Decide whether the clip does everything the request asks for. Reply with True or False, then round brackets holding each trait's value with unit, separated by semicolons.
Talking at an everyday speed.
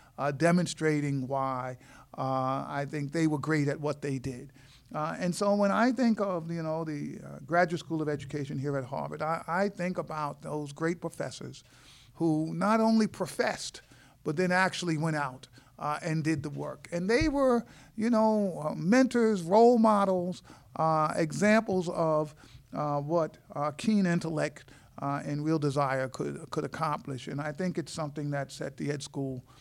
True (175 wpm)